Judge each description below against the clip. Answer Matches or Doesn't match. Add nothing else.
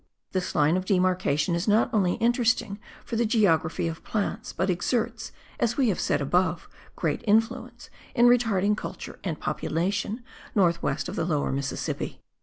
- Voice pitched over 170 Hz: Matches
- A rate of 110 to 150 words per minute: Doesn't match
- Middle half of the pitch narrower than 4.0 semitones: Doesn't match